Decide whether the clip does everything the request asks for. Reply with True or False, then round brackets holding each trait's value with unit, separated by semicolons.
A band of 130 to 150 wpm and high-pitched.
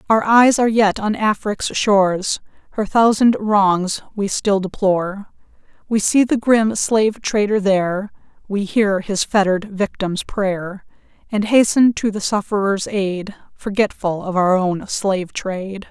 True (145 wpm; 200 Hz)